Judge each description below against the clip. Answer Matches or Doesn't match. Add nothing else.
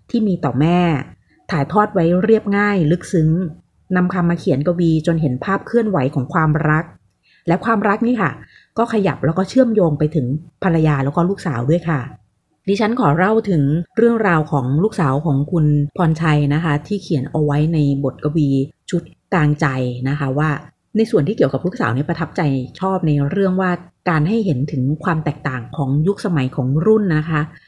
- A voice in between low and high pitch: Matches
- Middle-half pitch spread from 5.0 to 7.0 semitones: Doesn't match